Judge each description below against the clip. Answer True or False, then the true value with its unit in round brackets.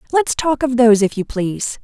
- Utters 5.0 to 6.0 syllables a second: False (6.3 syllables/s)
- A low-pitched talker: False (245 Hz)